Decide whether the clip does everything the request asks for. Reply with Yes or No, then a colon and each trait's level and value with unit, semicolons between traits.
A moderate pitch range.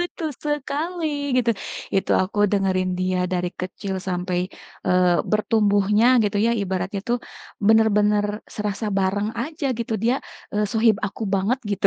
Yes: average, 3.5 semitones